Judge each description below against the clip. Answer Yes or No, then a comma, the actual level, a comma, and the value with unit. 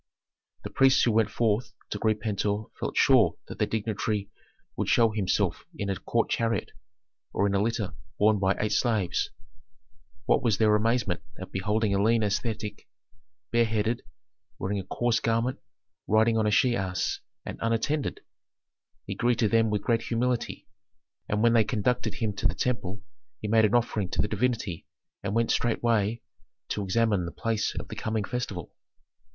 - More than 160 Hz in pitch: No, low, 110 Hz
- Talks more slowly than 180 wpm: Yes, average, 165 wpm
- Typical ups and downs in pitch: No, narrow, 2.1 semitones